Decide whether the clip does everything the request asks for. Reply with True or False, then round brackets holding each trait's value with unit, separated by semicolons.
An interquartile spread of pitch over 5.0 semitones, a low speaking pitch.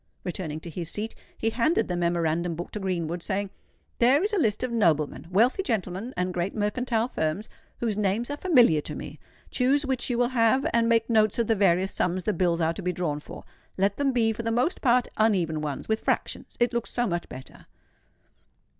False (5.4 semitones; 210 Hz)